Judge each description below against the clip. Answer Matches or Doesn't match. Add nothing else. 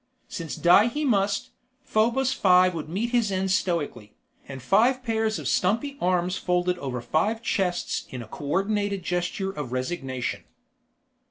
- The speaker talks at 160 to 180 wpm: Doesn't match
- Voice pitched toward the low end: Doesn't match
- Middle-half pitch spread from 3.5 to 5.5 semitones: Matches